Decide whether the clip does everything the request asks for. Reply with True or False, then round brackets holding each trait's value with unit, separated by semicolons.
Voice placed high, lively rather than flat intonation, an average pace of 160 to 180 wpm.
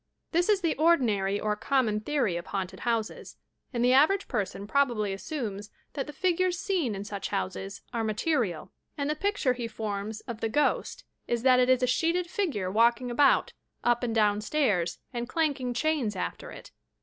True (240 Hz; 6.1 semitones; 175 wpm)